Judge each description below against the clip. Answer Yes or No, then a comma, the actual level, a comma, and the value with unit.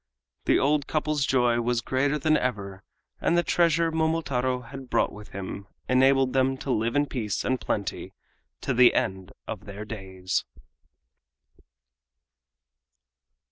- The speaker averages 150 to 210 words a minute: No, average, 140 wpm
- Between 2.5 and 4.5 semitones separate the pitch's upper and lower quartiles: No, average, 5.2 semitones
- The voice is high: No, low, 130 Hz